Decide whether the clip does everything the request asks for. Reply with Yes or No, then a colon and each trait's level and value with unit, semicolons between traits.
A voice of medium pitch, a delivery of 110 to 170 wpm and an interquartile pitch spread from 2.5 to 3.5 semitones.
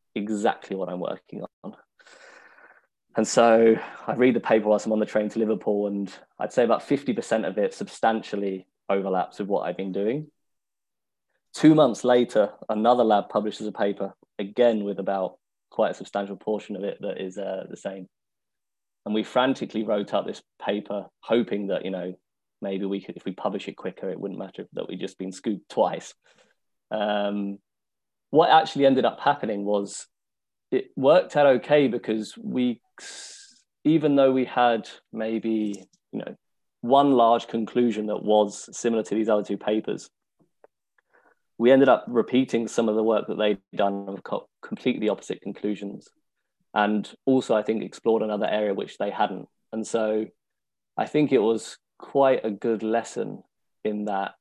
No: low, 110 Hz; average, 165 wpm; average, 3.1 semitones